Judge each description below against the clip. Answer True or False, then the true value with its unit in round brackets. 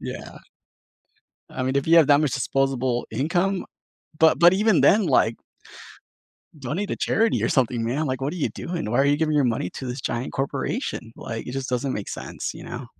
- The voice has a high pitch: False (135 Hz)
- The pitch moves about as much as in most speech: True (4.4 semitones)